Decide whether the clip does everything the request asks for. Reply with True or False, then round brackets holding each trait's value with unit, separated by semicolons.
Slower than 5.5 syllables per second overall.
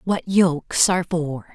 True (4.1 syllables/s)